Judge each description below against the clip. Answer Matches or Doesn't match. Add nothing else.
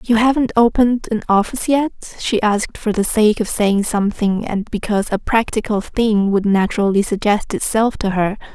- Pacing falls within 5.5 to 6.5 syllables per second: Doesn't match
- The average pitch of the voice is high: Matches